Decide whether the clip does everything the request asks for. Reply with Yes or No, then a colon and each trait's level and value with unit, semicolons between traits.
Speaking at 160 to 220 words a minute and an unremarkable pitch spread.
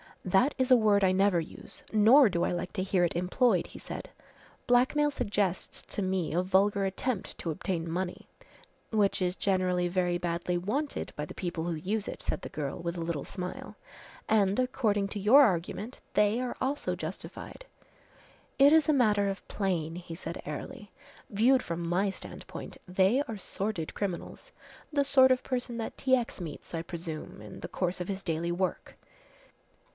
Yes: average, 180 wpm; average, 4.5 semitones